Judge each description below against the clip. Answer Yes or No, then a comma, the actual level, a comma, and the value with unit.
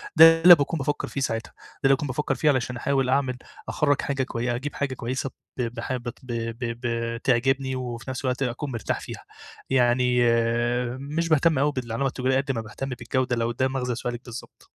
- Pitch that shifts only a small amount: Yes, narrow, 2.2 semitones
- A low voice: Yes, low, 130 Hz